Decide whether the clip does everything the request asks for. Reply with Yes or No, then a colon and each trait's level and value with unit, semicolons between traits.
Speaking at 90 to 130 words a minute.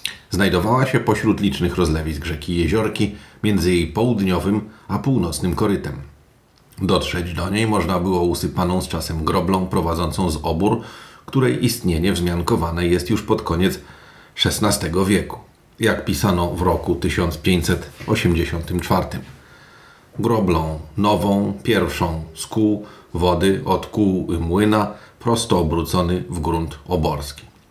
Yes: average, 115 wpm